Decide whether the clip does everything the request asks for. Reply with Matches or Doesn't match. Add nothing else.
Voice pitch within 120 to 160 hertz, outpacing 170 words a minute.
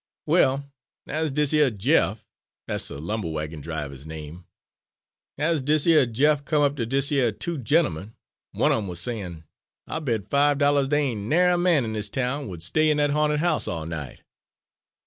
Matches